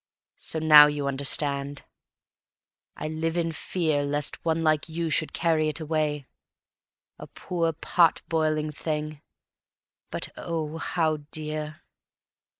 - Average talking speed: No, slow, 120 wpm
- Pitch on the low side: No, medium, 155 Hz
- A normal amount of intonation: No, narrow, 1.6 semitones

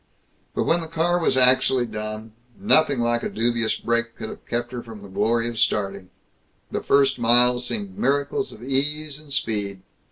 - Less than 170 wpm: No, average, 180 wpm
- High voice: No, low, 120 Hz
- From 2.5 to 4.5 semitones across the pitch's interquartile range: Yes, average, 4.1 semitones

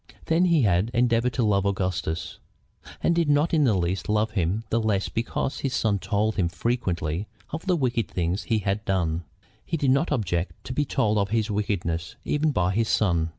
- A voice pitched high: No, low, 105 Hz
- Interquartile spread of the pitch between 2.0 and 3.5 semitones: No, average, 5.3 semitones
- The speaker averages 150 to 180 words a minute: No, average, 195 wpm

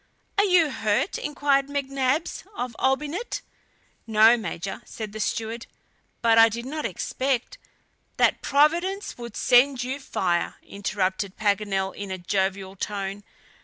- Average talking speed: No, slow, 130 wpm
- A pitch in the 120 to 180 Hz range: No, high, 235 Hz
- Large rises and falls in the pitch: Yes, wide, 5.7 semitones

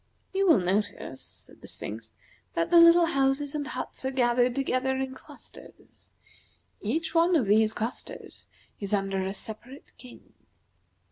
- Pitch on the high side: Yes, very high, 260 Hz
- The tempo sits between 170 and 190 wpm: No, average, 145 wpm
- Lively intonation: Yes, wide, 5.9 semitones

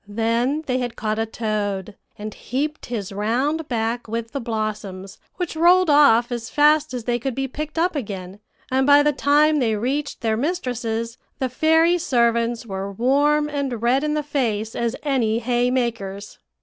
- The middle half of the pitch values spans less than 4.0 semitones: No, average, 4.6 semitones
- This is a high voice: Yes, high, 245 Hz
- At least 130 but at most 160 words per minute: No, average, 175 wpm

